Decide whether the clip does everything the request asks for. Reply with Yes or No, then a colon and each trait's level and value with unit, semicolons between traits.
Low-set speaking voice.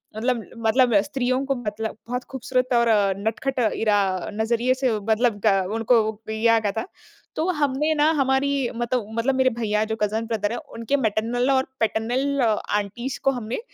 No: high, 240 Hz